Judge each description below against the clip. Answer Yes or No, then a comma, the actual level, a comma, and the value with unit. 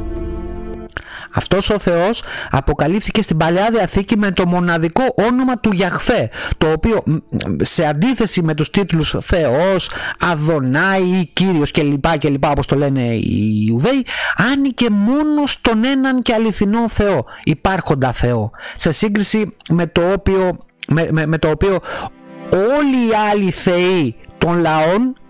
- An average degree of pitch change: No, wide, 5.7 semitones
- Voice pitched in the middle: Yes, medium, 180 Hz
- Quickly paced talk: No, average, 140 wpm